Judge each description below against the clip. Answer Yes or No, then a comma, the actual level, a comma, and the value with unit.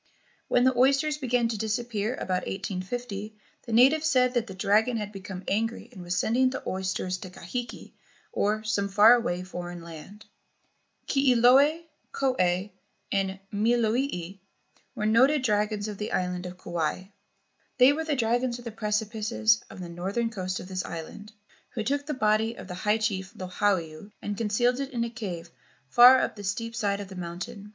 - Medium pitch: No, high, 215 Hz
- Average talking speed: Yes, average, 170 wpm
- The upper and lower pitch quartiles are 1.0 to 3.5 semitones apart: No, average, 4.4 semitones